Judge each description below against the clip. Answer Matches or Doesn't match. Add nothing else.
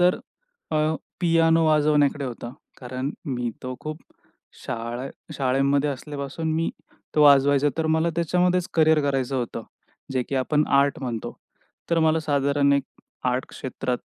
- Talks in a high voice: Doesn't match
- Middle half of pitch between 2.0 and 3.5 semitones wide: Matches